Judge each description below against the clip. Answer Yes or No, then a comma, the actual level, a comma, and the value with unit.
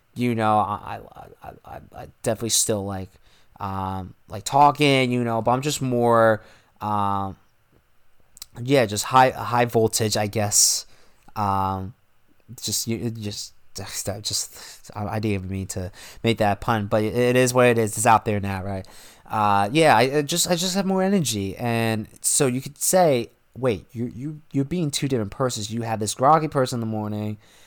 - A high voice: No, low, 115 Hz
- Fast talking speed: No, average, 175 wpm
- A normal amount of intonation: Yes, average, 3.6 semitones